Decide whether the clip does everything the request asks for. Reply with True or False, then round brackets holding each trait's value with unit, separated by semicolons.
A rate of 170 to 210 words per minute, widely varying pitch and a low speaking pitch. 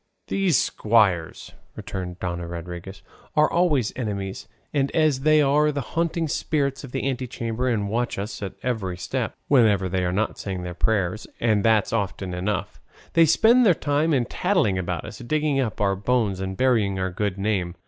True (180 wpm; 6.4 semitones; 110 Hz)